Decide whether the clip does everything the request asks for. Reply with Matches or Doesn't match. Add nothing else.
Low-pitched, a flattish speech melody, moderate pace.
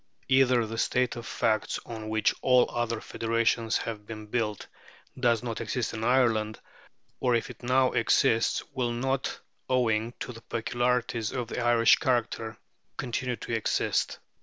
Matches